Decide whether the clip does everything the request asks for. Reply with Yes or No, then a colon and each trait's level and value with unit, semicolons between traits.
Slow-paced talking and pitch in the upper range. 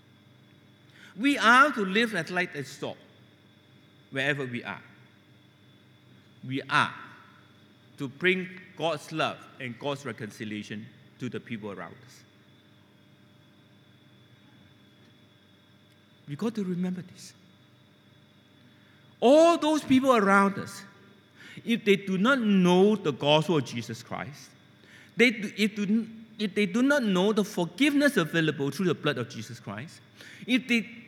No: slow, 125 wpm; medium, 150 Hz